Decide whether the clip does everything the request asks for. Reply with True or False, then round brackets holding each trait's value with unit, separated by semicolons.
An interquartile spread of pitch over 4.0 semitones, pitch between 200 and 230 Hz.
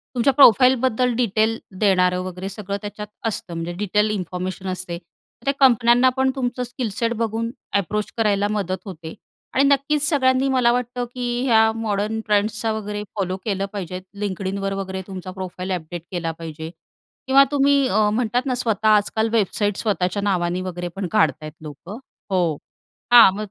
True (4.4 semitones; 210 Hz)